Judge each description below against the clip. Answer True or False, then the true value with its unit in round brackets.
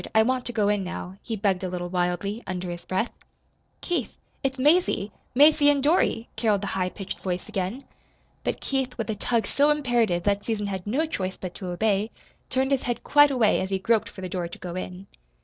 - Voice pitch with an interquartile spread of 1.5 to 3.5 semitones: False (5.5 semitones)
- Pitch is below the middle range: False (210 Hz)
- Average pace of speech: False (215 wpm)